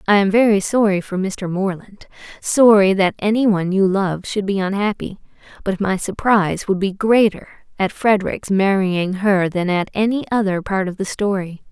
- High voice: Yes, high, 195 Hz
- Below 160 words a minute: No, average, 165 wpm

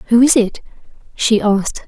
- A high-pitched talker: Yes, high, 220 Hz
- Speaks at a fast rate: No, average, 160 wpm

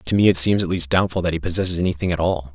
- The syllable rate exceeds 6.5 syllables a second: Yes, 7.4 syllables/s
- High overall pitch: No, very low, 85 Hz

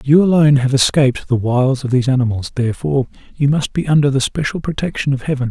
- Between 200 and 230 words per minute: Yes, fast, 205 wpm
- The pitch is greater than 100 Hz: Yes, low, 135 Hz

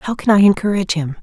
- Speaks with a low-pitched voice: No, high, 190 Hz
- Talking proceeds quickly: Yes, fast, 245 wpm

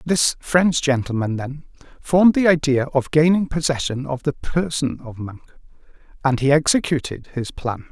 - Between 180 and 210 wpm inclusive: No, average, 150 wpm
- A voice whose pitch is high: No, medium, 145 Hz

